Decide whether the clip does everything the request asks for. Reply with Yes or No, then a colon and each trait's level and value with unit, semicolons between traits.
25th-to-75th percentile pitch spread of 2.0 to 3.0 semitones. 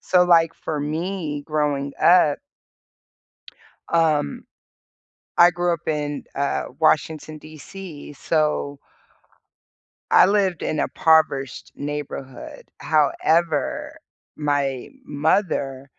Yes: average, 2.7 semitones